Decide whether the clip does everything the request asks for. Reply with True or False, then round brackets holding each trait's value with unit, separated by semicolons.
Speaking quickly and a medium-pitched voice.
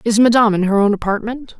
False (225 wpm; 220 Hz)